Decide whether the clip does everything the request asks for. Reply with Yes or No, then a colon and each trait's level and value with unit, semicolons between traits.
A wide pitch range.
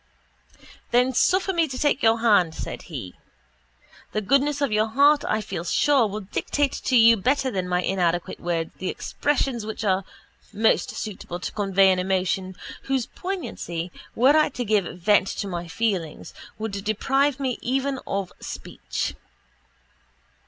Yes: wide, 6.1 semitones